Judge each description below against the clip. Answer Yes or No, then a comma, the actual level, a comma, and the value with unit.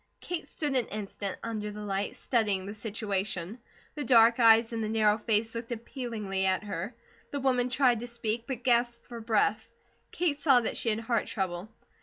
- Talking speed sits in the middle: Yes, average, 185 wpm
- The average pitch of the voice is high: Yes, high, 225 Hz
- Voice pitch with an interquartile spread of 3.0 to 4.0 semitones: No, narrow, 2.5 semitones